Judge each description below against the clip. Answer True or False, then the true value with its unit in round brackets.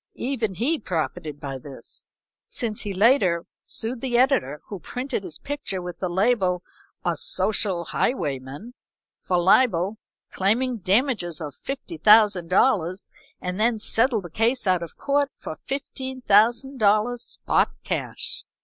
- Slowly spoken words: True (125 wpm)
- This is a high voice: True (210 Hz)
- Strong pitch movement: True (5.9 semitones)